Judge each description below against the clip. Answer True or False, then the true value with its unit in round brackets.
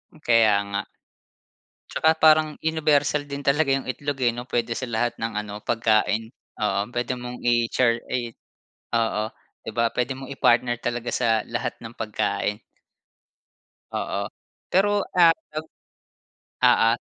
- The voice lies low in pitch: True (120 Hz)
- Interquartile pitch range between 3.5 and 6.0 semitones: True (3.8 semitones)